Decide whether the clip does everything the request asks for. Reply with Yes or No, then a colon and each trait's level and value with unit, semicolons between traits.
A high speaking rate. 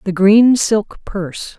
No: average, 150 wpm